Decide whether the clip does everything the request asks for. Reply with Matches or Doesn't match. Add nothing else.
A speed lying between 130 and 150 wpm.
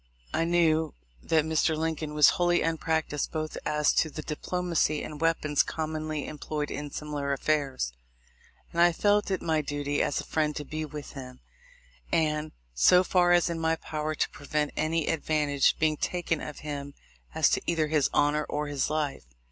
Doesn't match